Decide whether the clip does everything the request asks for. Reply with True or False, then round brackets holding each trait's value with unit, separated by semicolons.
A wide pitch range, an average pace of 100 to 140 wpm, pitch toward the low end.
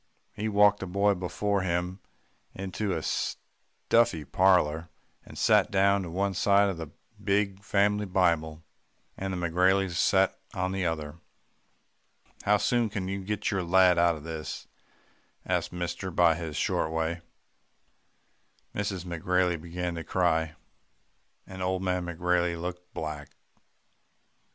False (2.5 semitones; 135 wpm; 90 Hz)